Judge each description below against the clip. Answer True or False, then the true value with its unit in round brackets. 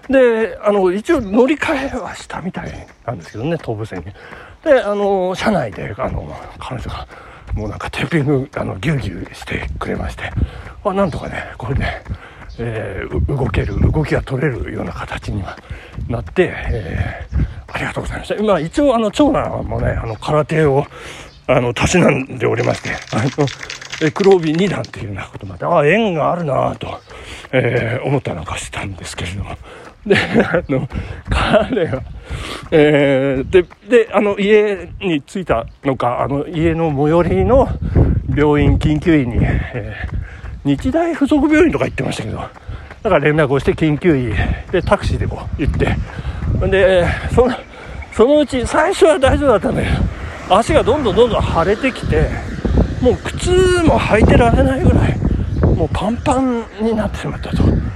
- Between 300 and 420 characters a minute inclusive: True (310 characters per minute)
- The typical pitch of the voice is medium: True (150 Hz)